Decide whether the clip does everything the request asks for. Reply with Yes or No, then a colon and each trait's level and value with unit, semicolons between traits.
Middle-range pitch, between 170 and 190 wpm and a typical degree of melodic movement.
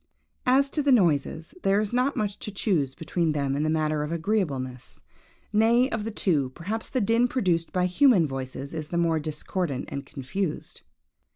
No: medium, 170 Hz; average, 180 wpm; wide, 6.4 semitones